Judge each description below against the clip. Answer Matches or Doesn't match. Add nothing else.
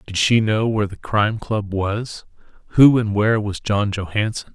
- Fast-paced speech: Doesn't match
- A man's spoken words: Matches